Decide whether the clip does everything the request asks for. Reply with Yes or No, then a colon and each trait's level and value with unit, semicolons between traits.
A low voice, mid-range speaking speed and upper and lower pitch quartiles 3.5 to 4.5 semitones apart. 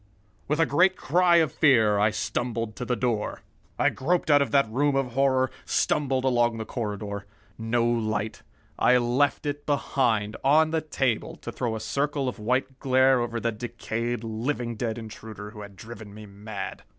Yes: low, 120 Hz; average, 175 wpm; average, 3.8 semitones